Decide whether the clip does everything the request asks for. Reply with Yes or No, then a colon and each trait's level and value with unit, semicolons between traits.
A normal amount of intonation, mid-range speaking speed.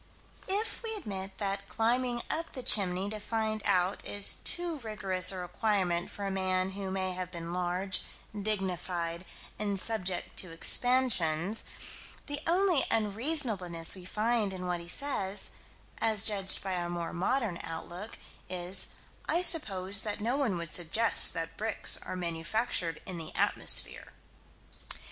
Yes: average, 3.9 semitones; average, 145 wpm